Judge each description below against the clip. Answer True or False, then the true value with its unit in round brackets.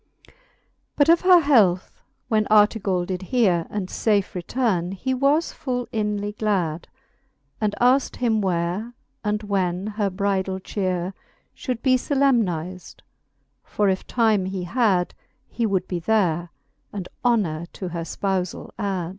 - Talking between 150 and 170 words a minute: False (135 wpm)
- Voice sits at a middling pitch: False (200 Hz)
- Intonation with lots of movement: False (4.0 semitones)